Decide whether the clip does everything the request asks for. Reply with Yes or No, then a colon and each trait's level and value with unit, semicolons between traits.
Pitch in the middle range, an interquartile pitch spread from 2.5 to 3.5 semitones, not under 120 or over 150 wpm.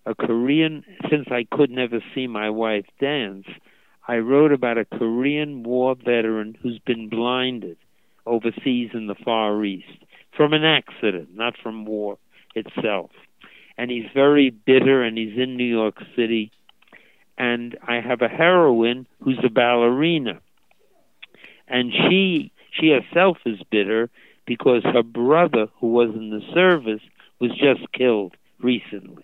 No: low, 120 Hz; average, 3.0 semitones; average, 140 wpm